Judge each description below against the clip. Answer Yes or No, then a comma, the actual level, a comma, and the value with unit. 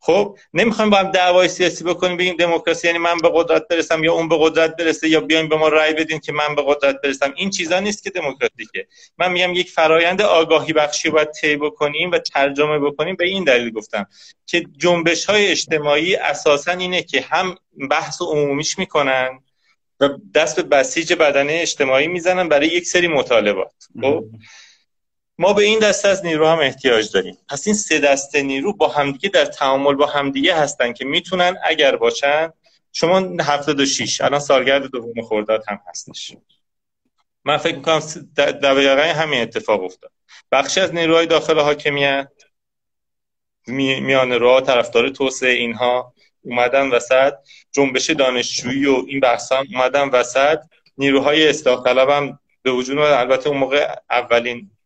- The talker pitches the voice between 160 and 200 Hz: No, medium, 150 Hz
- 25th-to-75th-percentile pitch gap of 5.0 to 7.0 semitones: No, average, 4.0 semitones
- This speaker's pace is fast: Yes, fast, 160 wpm